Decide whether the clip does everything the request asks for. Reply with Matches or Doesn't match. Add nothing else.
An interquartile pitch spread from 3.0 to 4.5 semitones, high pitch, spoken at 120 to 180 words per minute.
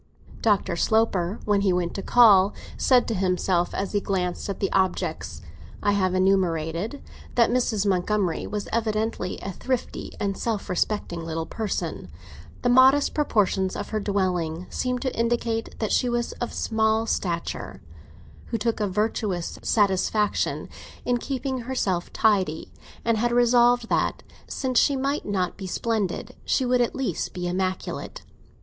Matches